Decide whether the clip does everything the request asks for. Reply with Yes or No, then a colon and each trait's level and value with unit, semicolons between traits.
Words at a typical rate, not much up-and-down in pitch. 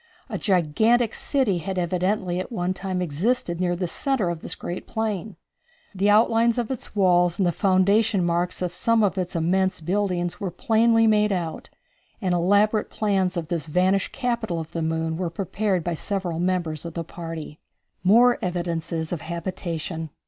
No: average, 170 wpm; average, 3.5 semitones